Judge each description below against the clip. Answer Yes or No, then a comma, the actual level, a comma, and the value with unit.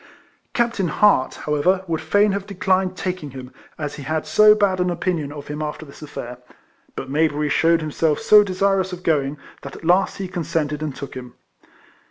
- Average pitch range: Yes, average, 4.2 semitones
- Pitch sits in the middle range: Yes, medium, 165 Hz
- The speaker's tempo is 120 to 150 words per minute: No, average, 185 wpm